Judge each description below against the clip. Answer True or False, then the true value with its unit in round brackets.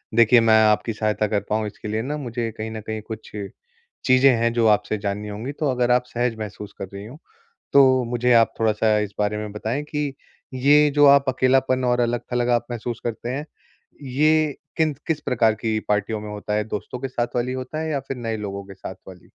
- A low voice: True (115 Hz)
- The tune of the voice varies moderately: True (3.2 semitones)